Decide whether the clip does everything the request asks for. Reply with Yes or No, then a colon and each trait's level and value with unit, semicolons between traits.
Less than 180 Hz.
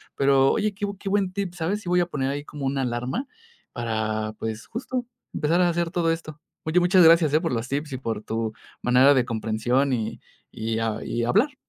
Yes: medium, 140 Hz